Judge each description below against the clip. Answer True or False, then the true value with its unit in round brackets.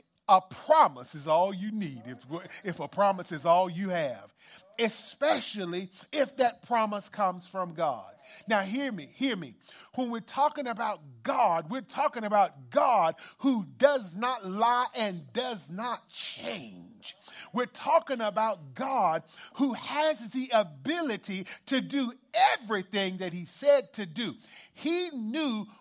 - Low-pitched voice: False (220 Hz)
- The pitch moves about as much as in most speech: False (6.0 semitones)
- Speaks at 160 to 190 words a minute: False (140 wpm)